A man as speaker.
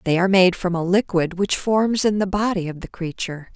No: female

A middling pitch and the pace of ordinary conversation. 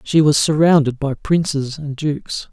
Yes: medium, 150 Hz; average, 165 wpm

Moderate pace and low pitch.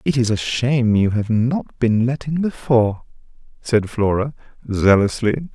Yes: average, 150 wpm; low, 120 Hz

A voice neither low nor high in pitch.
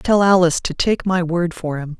Yes: medium, 175 Hz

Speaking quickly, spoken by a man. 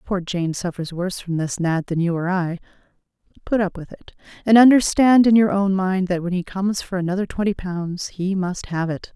No: fast, 215 wpm; female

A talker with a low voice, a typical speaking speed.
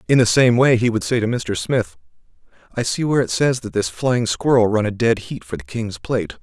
No: low, 115 Hz; fast, 250 wpm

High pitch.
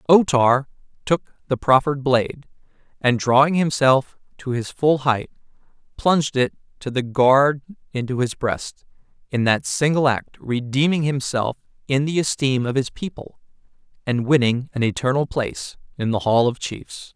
No: low, 135 Hz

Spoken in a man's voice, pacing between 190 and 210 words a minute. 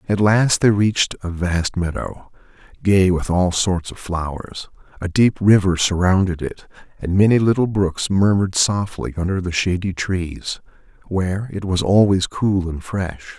No: male; average, 155 wpm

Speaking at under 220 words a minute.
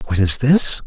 Yes: fast, 210 wpm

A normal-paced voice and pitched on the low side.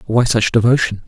Yes: average, 170 wpm; low, 115 Hz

